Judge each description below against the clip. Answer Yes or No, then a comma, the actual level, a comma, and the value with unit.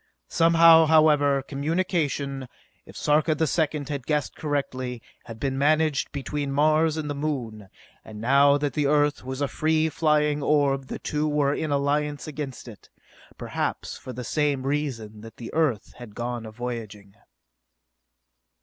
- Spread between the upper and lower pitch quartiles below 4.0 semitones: Yes, average, 2.8 semitones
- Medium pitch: Yes, medium, 145 Hz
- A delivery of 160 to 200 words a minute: No, average, 150 wpm